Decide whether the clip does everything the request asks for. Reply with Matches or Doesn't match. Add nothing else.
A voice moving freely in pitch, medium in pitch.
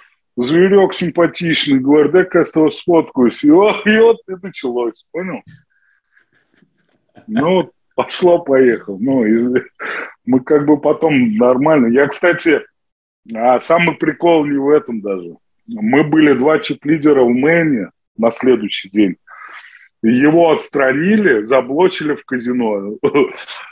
Matches